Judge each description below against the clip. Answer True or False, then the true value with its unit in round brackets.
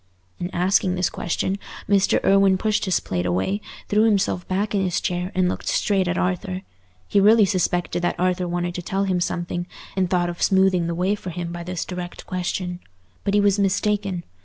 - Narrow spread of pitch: True (2.0 semitones)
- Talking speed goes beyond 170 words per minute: True (195 wpm)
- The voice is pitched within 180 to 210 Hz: True (185 Hz)